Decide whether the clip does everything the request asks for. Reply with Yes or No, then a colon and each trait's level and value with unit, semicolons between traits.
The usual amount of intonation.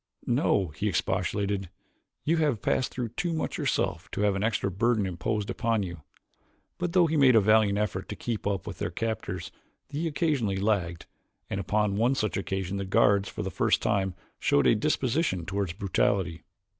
Yes: average, 3.6 semitones